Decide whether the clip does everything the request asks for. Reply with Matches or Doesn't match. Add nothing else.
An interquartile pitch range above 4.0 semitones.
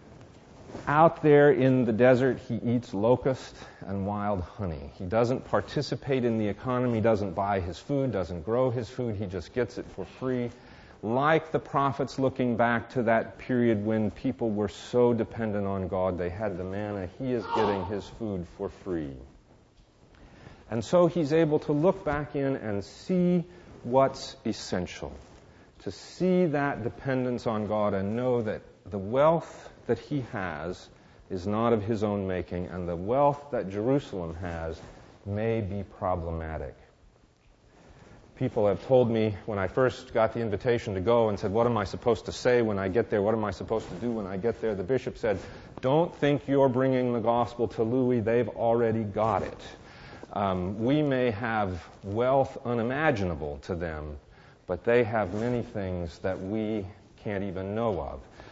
Matches